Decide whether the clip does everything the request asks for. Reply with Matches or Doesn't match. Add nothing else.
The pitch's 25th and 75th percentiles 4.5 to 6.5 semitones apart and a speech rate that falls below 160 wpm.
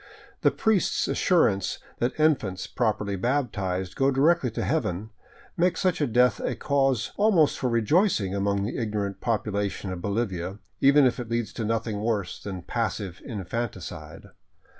Matches